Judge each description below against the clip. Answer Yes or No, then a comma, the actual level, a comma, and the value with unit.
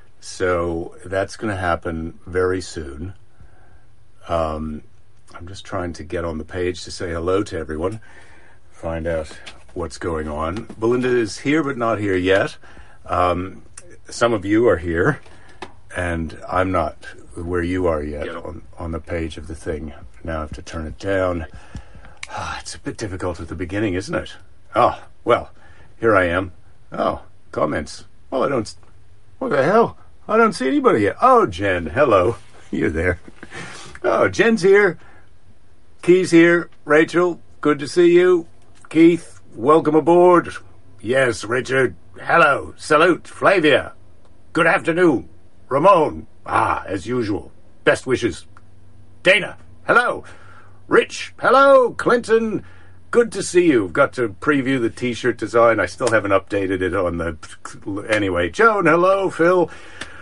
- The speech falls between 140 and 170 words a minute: Yes, average, 145 wpm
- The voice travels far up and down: Yes, wide, 8.4 semitones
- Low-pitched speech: Yes, very low, 95 Hz